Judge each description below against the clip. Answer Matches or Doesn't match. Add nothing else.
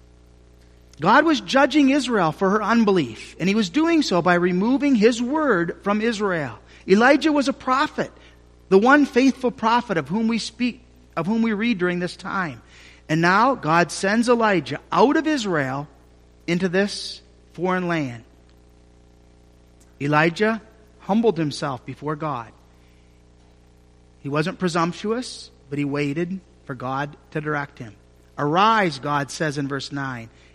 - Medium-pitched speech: Matches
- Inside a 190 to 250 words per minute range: Doesn't match